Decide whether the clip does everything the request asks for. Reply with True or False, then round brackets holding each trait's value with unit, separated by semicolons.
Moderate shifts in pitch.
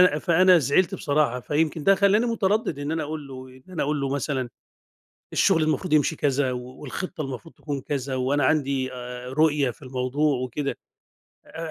True (3.7 semitones)